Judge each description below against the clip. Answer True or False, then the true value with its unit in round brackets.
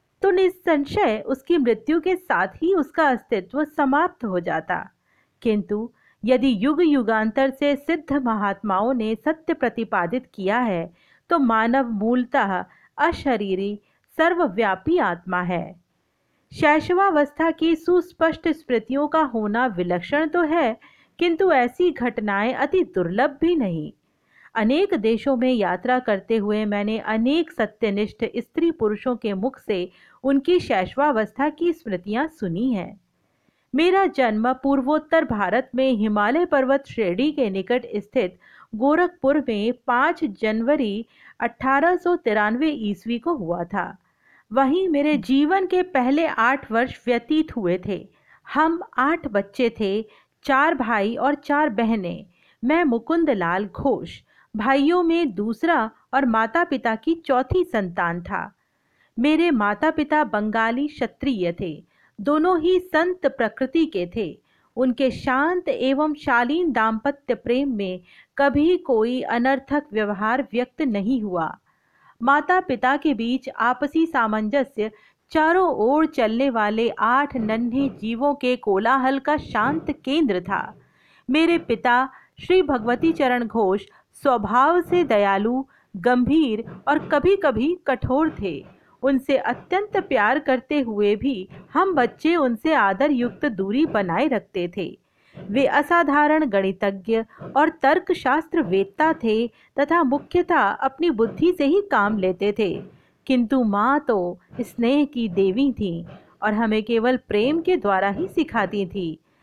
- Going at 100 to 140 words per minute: True (115 wpm)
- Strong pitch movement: True (5.9 semitones)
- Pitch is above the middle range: True (260 Hz)